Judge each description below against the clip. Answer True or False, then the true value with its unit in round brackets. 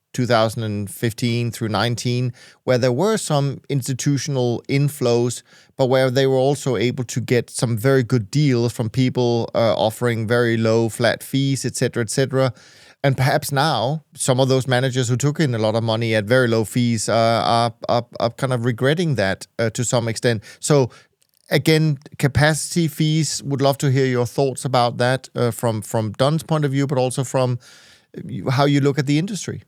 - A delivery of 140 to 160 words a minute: False (185 wpm)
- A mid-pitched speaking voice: False (130 Hz)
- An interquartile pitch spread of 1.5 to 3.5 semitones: True (2.8 semitones)